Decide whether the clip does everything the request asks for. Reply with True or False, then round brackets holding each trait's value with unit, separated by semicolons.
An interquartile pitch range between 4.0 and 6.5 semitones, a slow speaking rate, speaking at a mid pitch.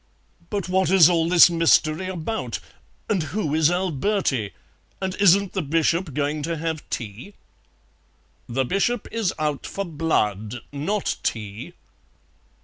True (4.7 semitones; 130 wpm; 165 Hz)